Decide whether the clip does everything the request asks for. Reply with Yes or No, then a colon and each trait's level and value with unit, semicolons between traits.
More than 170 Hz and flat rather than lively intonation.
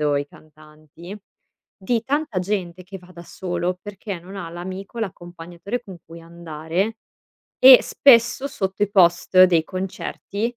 No: medium, 185 Hz; average, 3.2 semitones